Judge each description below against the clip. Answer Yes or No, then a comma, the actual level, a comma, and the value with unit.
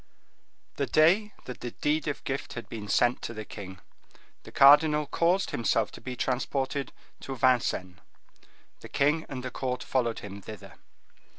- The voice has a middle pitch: No, low, 130 Hz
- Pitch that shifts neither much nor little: Yes, average, 4.2 semitones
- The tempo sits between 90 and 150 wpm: No, average, 160 wpm